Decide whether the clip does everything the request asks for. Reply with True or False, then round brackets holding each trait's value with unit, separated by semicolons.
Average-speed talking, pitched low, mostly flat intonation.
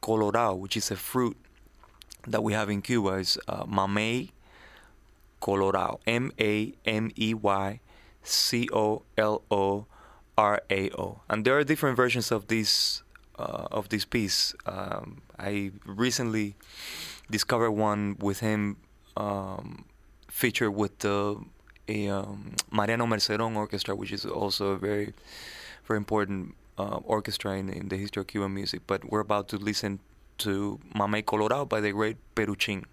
True (145 wpm; 105 Hz; 1.8 semitones)